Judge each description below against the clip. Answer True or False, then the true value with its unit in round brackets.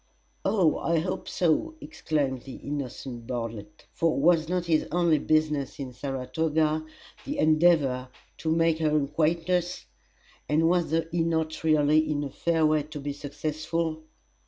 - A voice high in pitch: False (155 Hz)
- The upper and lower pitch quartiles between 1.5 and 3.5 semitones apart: True (2.4 semitones)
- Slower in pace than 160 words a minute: True (140 wpm)